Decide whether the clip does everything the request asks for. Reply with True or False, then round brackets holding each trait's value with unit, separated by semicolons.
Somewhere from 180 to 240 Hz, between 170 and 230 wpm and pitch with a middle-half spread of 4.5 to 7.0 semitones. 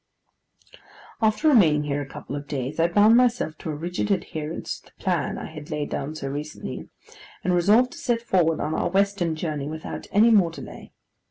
False (165 Hz; 190 wpm; 5.3 semitones)